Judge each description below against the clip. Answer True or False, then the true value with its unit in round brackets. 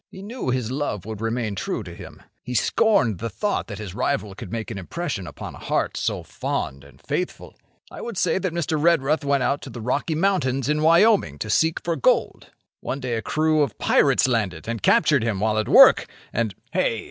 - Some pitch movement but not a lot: False (6.7 semitones)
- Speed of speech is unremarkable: False (210 wpm)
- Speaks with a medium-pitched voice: False (125 Hz)